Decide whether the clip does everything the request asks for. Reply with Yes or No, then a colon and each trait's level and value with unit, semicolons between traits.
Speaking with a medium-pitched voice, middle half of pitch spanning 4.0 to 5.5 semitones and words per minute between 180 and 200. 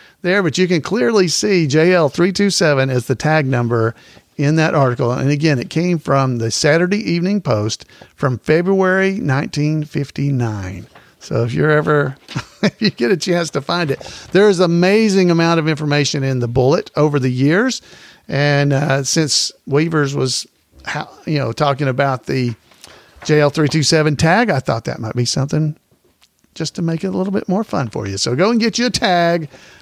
Yes: medium, 150 Hz; average, 4.7 semitones; average, 190 wpm